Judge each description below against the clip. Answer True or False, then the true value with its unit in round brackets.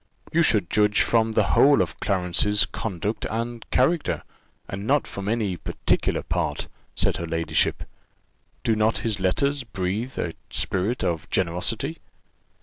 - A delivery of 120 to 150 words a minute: True (140 wpm)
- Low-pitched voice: True (105 Hz)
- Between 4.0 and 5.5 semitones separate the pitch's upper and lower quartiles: True (4.5 semitones)